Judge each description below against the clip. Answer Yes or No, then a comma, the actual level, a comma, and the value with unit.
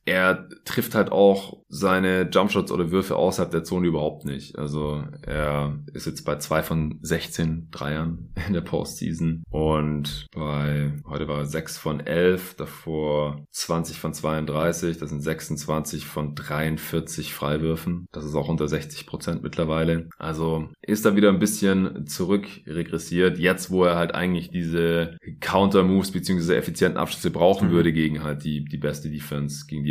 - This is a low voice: Yes, very low, 80 Hz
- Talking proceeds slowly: No, average, 155 wpm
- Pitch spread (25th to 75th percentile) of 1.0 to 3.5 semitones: Yes, narrow, 2.6 semitones